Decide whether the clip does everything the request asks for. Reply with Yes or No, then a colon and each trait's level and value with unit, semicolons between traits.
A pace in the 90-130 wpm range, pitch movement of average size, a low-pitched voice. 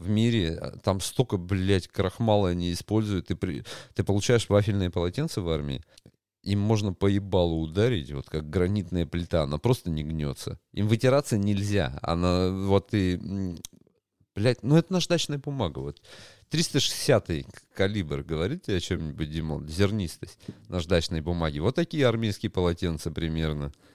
No: average, 140 wpm; average, 4.3 semitones; very low, 95 Hz